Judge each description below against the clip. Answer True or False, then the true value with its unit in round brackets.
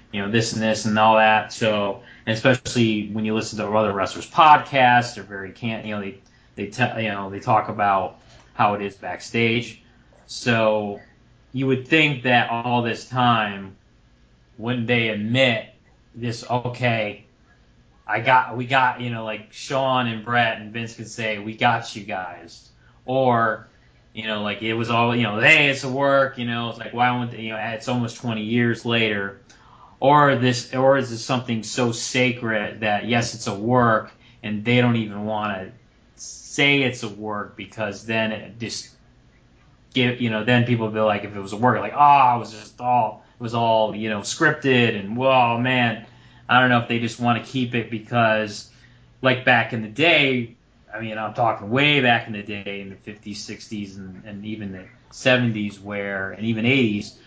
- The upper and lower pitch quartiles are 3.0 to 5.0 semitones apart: False (2.5 semitones)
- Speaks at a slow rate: False (195 wpm)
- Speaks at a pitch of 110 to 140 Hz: True (115 Hz)